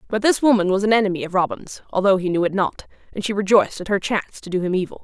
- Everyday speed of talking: No, fast, 275 wpm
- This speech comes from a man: No, female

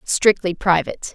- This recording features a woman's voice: Yes, female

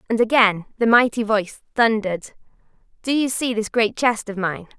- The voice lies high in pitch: Yes, high, 220 Hz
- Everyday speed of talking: Yes, average, 175 wpm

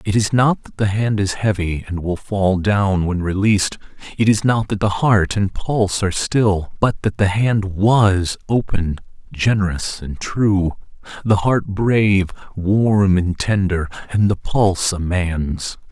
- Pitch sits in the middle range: No, low, 100 Hz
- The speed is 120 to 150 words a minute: No, average, 165 wpm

